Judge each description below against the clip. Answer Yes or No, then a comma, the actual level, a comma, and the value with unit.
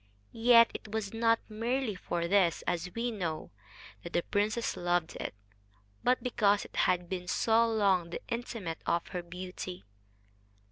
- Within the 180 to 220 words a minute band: No, average, 150 wpm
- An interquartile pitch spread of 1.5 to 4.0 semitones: No, average, 4.5 semitones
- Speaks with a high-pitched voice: Yes, high, 200 Hz